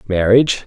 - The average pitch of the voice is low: Yes, low, 110 Hz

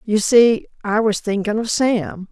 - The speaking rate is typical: Yes, average, 180 wpm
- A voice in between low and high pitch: No, high, 215 Hz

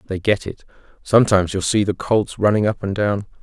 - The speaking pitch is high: No, low, 100 Hz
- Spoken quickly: Yes, fast, 210 wpm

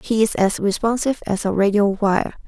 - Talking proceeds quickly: No, average, 195 wpm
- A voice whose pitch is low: No, high, 210 Hz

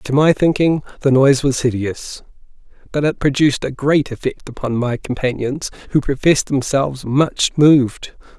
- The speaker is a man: Yes, male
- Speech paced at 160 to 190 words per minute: No, average, 150 wpm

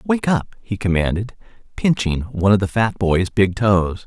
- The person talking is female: No, male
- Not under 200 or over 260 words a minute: No, average, 175 wpm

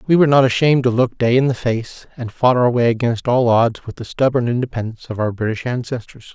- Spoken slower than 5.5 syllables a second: No, 6.1 syllables/s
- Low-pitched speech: Yes, low, 120 Hz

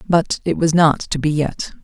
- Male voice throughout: No, female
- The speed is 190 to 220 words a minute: No, fast, 230 wpm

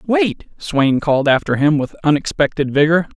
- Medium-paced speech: Yes, average, 150 wpm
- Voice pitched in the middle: Yes, medium, 155 Hz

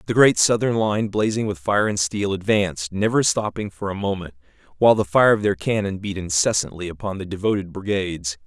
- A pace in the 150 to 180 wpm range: No, average, 190 wpm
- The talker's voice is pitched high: No, low, 100 Hz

